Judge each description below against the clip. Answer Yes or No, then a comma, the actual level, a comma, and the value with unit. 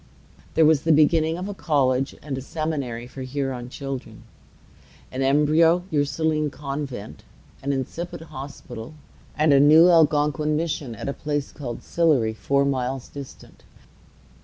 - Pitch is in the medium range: Yes, medium, 145 Hz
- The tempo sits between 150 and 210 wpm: No, slow, 135 wpm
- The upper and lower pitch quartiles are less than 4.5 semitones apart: Yes, average, 2.7 semitones